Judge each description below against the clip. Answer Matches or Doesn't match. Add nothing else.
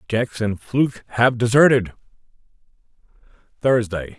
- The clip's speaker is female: Doesn't match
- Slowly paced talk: Matches